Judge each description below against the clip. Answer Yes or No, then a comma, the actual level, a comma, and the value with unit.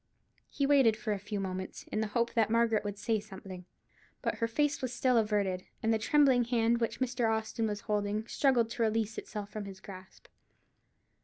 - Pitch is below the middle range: No, high, 220 Hz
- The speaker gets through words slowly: No, average, 190 wpm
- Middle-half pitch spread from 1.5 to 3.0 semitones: Yes, narrow, 2.4 semitones